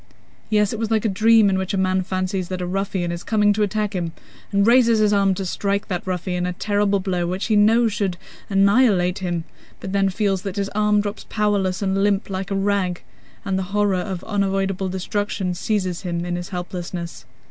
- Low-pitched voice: No, high, 195 Hz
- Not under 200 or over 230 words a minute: Yes, fast, 205 wpm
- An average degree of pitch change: No, narrow, 2.1 semitones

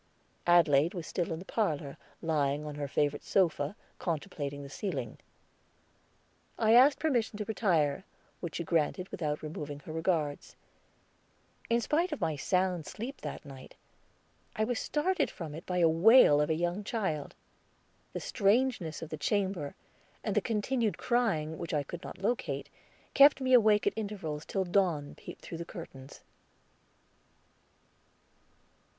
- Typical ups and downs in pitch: No, wide, 6.2 semitones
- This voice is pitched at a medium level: Yes, medium, 175 Hz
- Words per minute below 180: Yes, average, 145 wpm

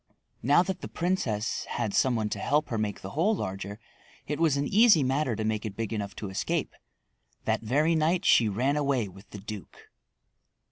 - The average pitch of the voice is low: Yes, low, 120 Hz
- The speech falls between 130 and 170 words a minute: No, average, 195 wpm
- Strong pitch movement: Yes, wide, 6.5 semitones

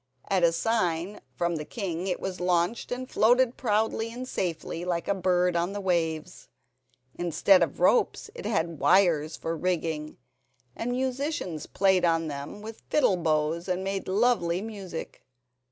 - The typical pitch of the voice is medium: Yes, medium, 180 Hz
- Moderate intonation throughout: Yes, average, 4.1 semitones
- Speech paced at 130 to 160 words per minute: Yes, average, 155 wpm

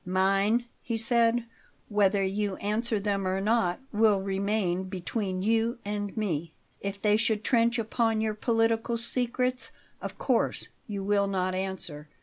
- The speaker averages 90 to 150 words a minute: Yes, average, 140 wpm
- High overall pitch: Yes, high, 210 Hz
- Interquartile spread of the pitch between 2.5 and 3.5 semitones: Yes, average, 2.8 semitones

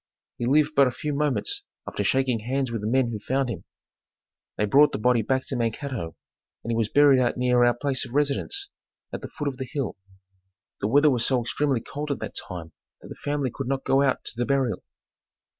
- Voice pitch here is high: No, low, 130 Hz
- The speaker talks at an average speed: No, fast, 220 wpm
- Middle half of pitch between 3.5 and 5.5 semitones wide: No, average, 3.1 semitones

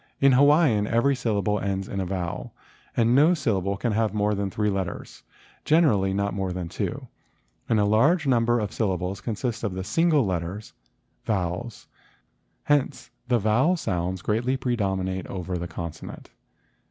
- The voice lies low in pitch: Yes, low, 105 Hz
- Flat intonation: No, average, 4.3 semitones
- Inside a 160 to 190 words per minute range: No, average, 150 wpm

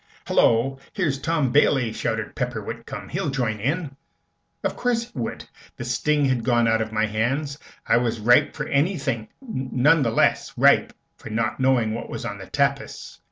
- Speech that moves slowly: No, average, 180 wpm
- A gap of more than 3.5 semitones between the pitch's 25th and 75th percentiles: Yes, average, 4.2 semitones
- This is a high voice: No, low, 125 Hz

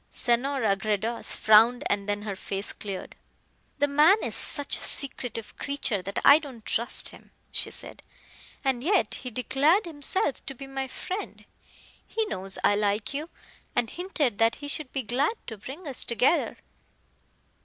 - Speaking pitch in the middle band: No, very high, 255 Hz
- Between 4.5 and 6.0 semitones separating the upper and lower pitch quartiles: Yes, average, 5.1 semitones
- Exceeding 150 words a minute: Yes, average, 160 wpm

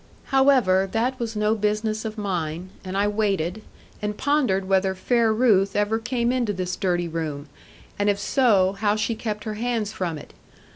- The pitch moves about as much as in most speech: Yes, average, 3.0 semitones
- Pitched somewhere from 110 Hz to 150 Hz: No, high, 210 Hz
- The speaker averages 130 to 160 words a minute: No, average, 175 wpm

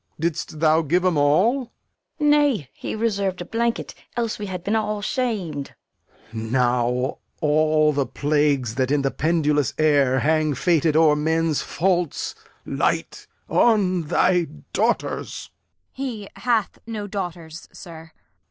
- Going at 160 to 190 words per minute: No, average, 140 wpm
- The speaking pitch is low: No, medium, 165 Hz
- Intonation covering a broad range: Yes, wide, 5.7 semitones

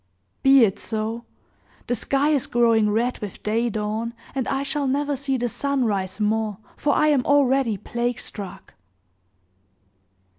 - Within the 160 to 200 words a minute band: No, average, 150 wpm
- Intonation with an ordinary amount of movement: Yes, average, 4.0 semitones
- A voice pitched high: Yes, high, 240 Hz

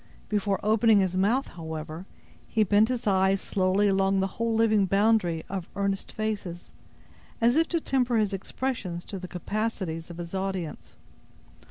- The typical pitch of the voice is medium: No, high, 195 Hz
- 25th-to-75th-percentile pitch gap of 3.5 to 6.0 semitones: No, average, 3.1 semitones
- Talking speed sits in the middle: Yes, average, 155 wpm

